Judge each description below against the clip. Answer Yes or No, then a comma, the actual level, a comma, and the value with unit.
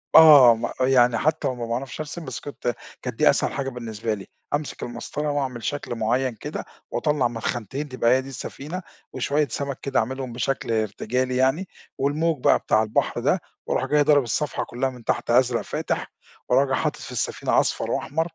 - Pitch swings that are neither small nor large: Yes, average, 3.3 semitones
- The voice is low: Yes, low, 130 Hz